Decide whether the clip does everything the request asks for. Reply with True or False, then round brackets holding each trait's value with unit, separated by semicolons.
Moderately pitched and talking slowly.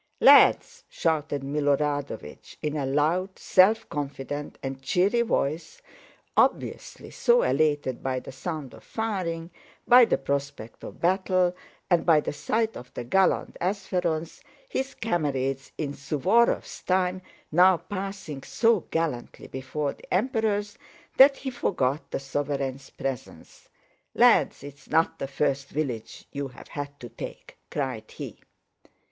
True (155 Hz; 130 wpm)